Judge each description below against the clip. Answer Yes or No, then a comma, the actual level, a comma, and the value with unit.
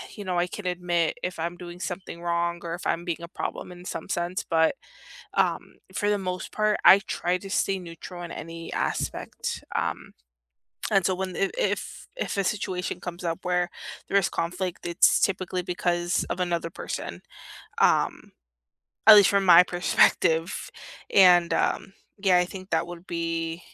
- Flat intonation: Yes, narrow, 1.6 semitones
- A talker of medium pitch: Yes, medium, 180 Hz